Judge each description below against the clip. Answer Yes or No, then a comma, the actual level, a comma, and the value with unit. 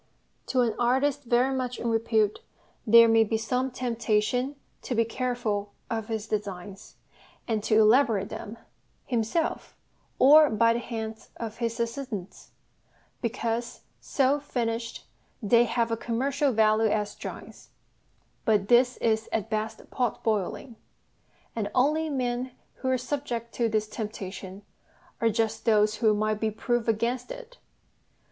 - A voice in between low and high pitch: No, high, 230 Hz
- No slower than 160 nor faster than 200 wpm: No, average, 140 wpm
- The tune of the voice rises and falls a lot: No, narrow, 2.5 semitones